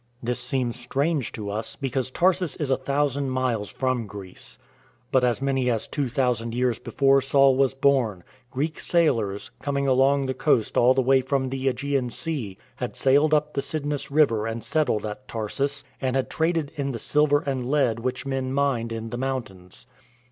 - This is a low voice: Yes, low, 130 Hz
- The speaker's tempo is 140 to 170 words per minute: No, average, 185 wpm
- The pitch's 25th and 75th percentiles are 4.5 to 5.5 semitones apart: No, average, 2.8 semitones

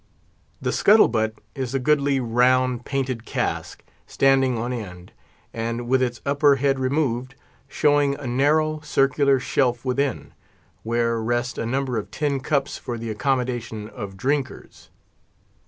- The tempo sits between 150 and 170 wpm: No, average, 140 wpm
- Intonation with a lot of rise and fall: No, average, 2.7 semitones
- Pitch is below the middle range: Yes, low, 130 Hz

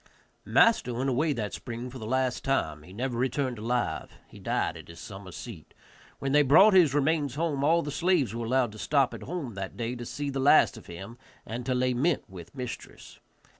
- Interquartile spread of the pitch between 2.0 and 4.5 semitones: Yes, average, 3.8 semitones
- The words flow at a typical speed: No, fast, 210 wpm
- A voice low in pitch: Yes, low, 125 Hz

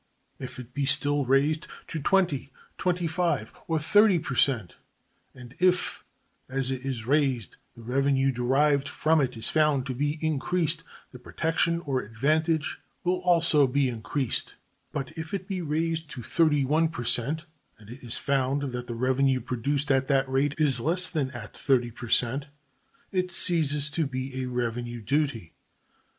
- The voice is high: No, medium, 140 Hz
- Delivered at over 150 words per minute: Yes, average, 160 wpm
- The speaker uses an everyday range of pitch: Yes, average, 3.8 semitones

